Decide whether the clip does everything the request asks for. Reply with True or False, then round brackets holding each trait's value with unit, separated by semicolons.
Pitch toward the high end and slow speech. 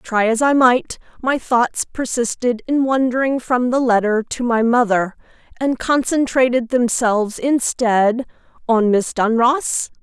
True (245 Hz; 125 wpm)